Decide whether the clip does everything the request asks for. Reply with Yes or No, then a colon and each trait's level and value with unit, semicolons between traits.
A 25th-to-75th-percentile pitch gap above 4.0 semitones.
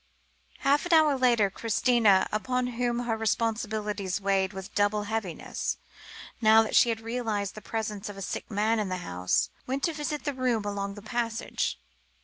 No: average, 3.1 semitones